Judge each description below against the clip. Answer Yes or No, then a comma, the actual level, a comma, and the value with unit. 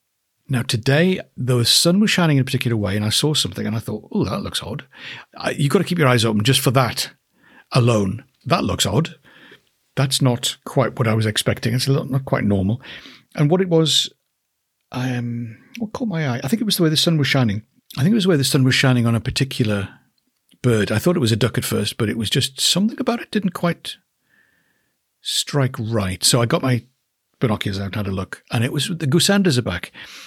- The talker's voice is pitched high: No, low, 130 Hz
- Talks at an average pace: No, fast, 230 wpm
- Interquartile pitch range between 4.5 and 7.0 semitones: Yes, average, 5.0 semitones